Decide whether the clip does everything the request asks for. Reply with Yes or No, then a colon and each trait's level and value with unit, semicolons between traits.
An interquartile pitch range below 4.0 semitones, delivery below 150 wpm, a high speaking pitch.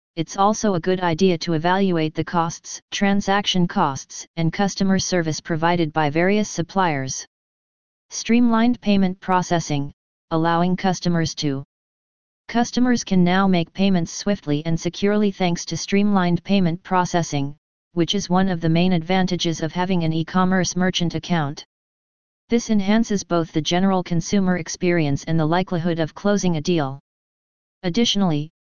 No: average, 2.9 semitones; average, 140 wpm; medium, 180 Hz